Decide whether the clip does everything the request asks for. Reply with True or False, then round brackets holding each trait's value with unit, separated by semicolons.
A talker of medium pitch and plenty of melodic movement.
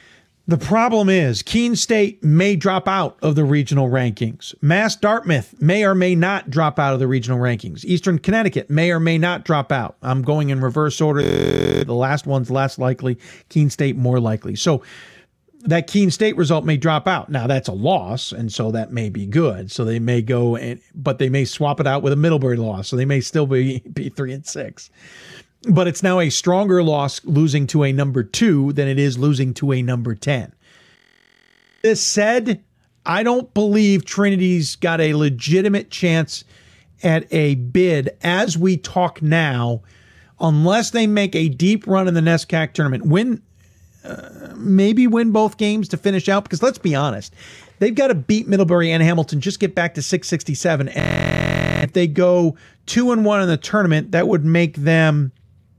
True (160 Hz; 6.0 semitones)